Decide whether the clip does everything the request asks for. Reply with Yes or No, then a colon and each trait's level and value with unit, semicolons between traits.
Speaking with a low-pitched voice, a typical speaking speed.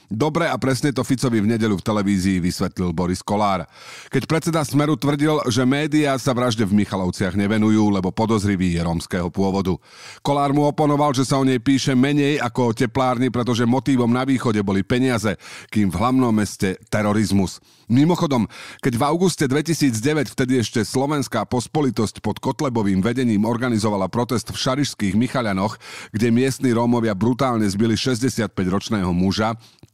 Yes: low, 120 Hz; average, 150 wpm